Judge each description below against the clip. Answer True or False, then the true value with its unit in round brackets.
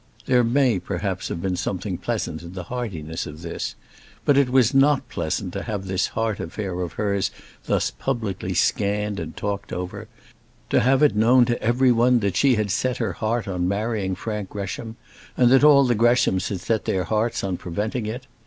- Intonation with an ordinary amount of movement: True (4.5 semitones)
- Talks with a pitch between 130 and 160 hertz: False (105 Hz)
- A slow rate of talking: False (190 wpm)